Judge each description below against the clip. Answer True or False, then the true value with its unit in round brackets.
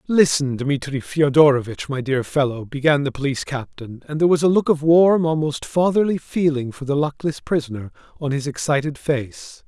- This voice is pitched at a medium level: True (145 Hz)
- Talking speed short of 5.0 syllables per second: False (5.2 syllables/s)